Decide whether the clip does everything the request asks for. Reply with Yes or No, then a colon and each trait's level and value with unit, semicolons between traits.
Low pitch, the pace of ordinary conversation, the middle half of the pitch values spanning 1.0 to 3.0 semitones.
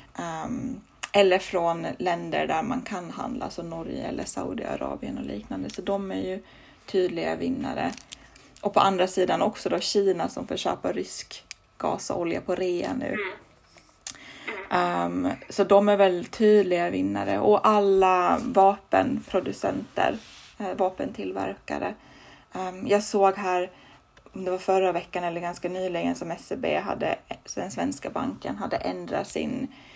No: medium, 185 Hz; average, 135 wpm; narrow, 2.4 semitones